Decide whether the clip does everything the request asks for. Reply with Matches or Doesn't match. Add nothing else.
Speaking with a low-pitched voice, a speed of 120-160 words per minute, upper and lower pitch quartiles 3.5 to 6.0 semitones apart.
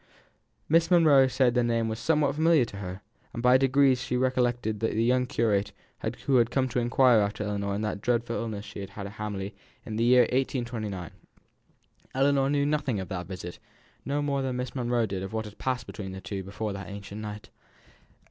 Doesn't match